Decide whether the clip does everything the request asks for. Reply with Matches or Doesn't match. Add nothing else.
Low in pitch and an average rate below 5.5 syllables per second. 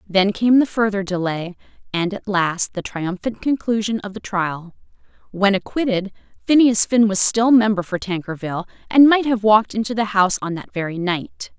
Doesn't match